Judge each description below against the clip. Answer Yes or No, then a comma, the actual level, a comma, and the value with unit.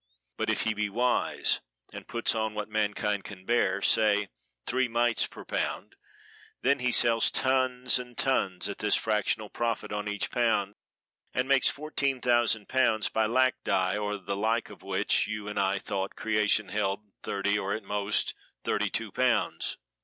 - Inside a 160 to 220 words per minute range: Yes, average, 170 wpm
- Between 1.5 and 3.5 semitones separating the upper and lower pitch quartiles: Yes, average, 2.8 semitones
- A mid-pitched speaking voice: No, low, 110 Hz